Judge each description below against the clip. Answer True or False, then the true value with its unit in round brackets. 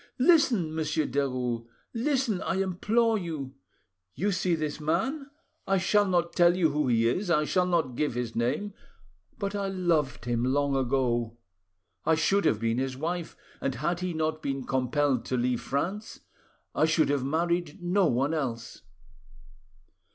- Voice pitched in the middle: True (155 Hz)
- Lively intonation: True (5.7 semitones)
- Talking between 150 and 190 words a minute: True (160 wpm)